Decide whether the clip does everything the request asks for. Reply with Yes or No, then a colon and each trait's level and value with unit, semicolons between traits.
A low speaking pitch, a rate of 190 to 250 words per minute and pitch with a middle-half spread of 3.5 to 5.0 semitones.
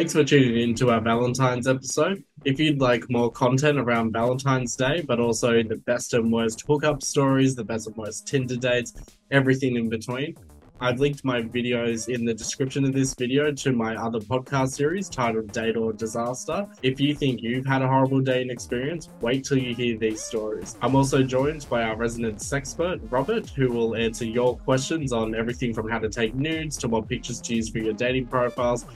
No: low, 125 Hz; average, 200 wpm; average, 2.8 semitones